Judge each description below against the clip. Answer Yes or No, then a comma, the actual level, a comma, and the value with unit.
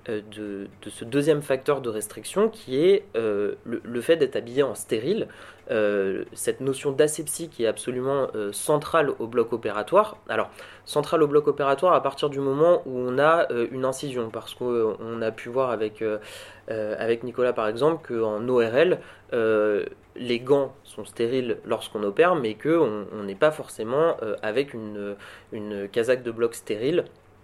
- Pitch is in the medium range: No, low, 125 Hz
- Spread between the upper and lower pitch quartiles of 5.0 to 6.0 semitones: Yes, average, 5.3 semitones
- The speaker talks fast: No, average, 170 wpm